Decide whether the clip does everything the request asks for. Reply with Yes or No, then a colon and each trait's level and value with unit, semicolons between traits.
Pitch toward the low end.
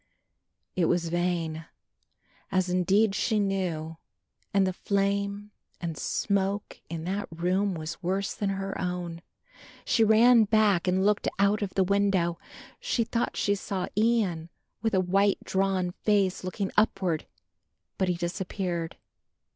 No: high, 190 Hz